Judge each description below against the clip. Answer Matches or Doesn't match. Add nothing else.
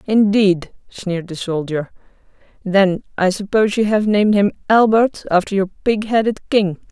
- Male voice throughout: Doesn't match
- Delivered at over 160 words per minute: Doesn't match